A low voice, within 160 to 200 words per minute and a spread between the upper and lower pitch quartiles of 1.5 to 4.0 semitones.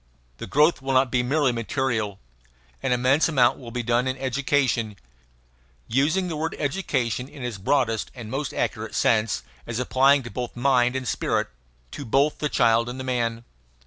Yes: low, 130 Hz; average, 175 wpm; average, 2.8 semitones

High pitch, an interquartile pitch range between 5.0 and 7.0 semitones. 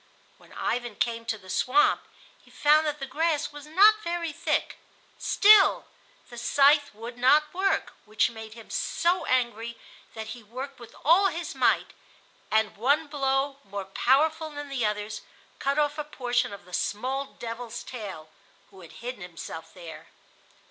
Yes: very high, 255 Hz; wide, 5.5 semitones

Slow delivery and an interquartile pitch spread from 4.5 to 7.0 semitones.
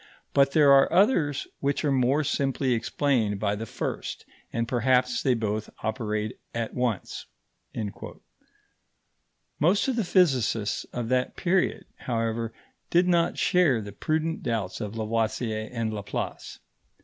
Yes: slow, 130 wpm; average, 4.8 semitones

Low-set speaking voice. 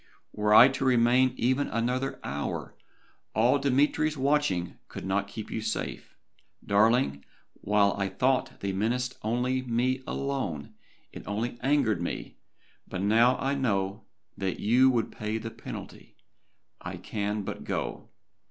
Yes: low, 115 Hz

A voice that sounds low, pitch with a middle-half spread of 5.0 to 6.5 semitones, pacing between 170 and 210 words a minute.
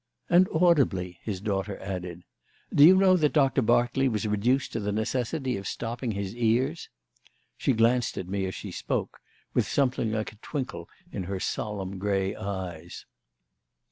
No: low, 110 Hz; average, 5.3 semitones; average, 160 wpm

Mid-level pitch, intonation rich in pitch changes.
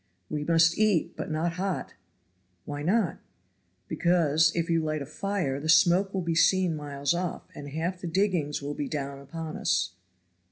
No: medium, 165 Hz; average, 3.4 semitones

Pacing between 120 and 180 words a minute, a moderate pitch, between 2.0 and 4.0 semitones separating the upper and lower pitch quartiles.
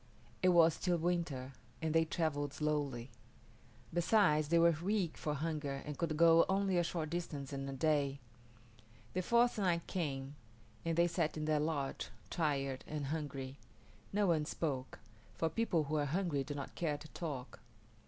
Yes: average, 165 wpm; medium, 155 Hz; average, 3.2 semitones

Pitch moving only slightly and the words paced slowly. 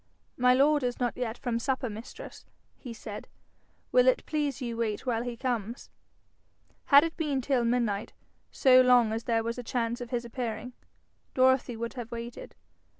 No: narrow, 1.8 semitones; average, 170 wpm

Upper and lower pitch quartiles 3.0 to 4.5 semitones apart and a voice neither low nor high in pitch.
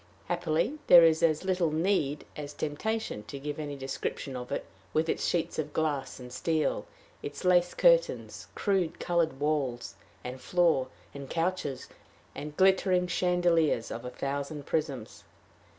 Yes: average, 4.2 semitones; medium, 155 Hz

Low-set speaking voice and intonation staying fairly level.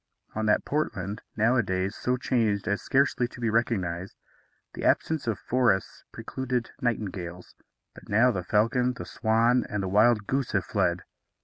No: low, 110 Hz; average, 3.9 semitones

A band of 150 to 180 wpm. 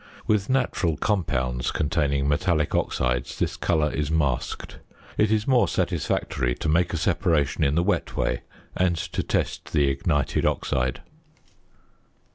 No: slow, 135 wpm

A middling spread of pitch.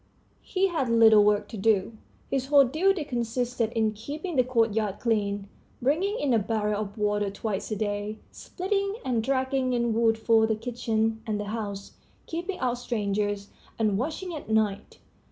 Yes: average, 3.8 semitones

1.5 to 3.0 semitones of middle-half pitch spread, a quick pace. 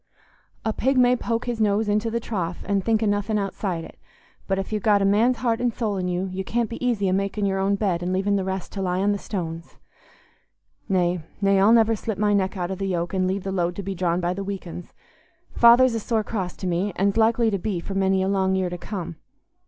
Yes: average, 2.7 semitones; fast, 255 wpm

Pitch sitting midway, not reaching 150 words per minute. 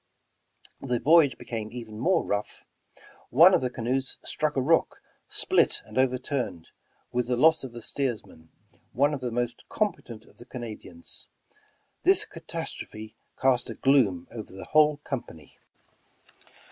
No: low, 125 Hz; average, 140 wpm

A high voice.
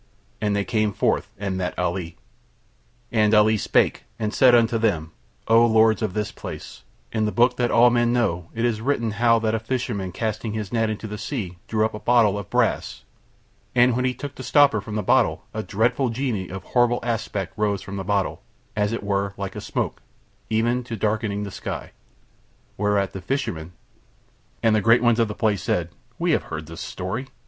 No: low, 110 Hz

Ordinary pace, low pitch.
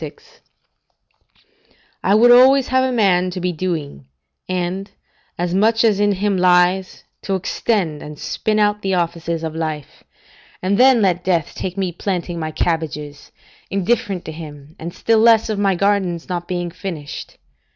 No: average, 160 wpm; medium, 185 Hz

